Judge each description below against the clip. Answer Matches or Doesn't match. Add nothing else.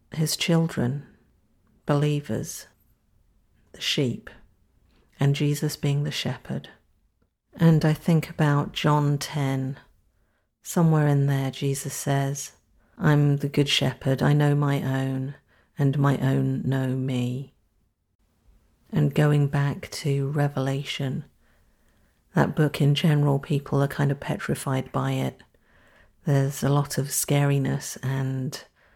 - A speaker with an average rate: Doesn't match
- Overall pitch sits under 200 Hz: Matches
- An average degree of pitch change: Doesn't match